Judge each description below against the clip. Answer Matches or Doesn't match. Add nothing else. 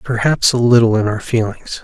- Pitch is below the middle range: Matches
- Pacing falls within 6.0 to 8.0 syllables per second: Doesn't match